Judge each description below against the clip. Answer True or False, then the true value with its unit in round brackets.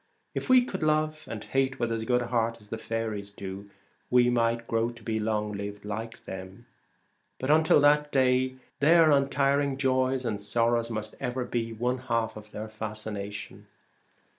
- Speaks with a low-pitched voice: True (115 Hz)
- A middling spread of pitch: True (3.5 semitones)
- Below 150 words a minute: False (170 wpm)